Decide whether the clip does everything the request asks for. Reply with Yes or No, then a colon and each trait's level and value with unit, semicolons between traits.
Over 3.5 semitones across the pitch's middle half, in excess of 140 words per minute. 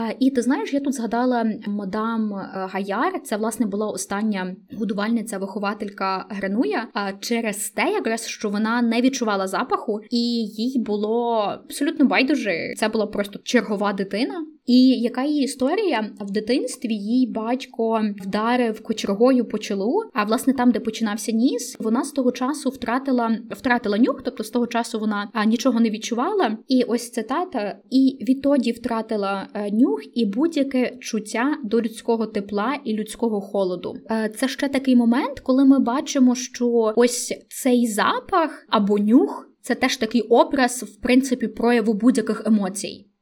No: average, 3.1 semitones; average, 150 wpm